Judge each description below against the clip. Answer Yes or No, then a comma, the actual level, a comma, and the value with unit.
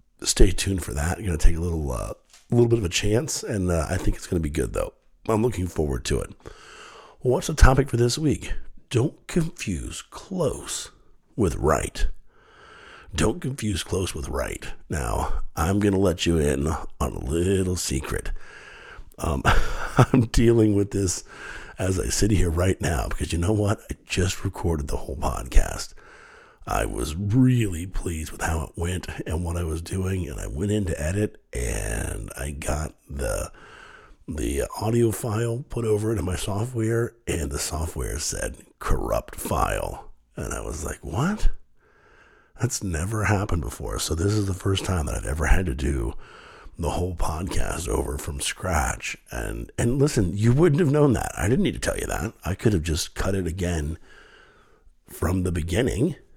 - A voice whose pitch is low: Yes, very low, 90 Hz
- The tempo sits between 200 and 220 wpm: No, average, 180 wpm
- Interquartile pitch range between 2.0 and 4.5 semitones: No, average, 4.9 semitones